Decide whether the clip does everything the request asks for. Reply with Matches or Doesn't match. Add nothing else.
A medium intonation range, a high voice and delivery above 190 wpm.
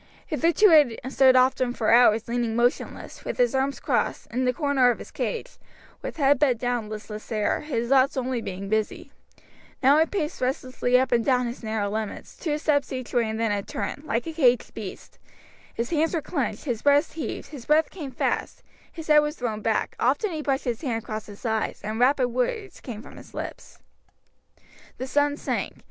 Matches